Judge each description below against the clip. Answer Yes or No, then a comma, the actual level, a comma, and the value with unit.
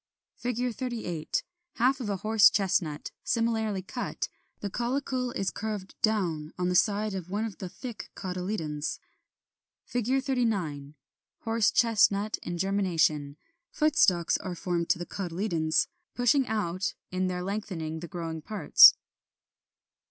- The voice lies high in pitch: Yes, high, 195 Hz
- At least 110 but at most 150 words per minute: Yes, slow, 135 wpm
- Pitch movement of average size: Yes, average, 4.4 semitones